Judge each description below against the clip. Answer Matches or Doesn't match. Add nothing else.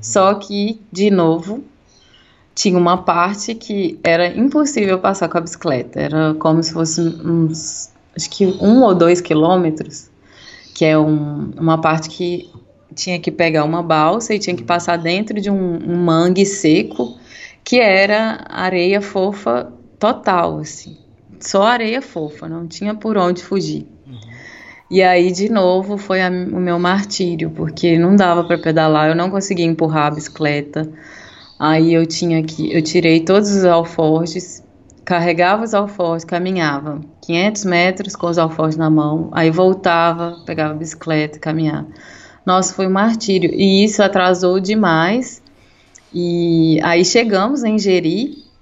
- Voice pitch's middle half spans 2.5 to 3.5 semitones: Matches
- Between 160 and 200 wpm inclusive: Doesn't match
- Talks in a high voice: Doesn't match